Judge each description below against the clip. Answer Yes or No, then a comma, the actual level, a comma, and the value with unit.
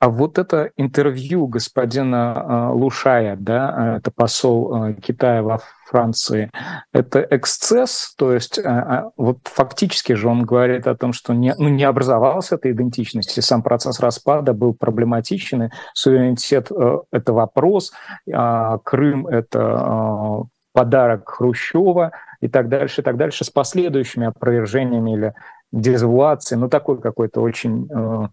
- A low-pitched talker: Yes, low, 125 Hz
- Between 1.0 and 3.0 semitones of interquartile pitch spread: Yes, narrow, 2.6 semitones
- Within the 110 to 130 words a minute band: Yes, average, 125 wpm